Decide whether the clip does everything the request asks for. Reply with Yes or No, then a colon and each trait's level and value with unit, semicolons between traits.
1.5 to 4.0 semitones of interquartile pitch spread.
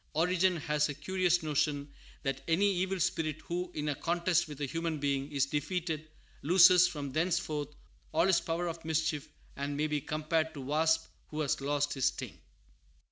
Yes: average, 2.8 semitones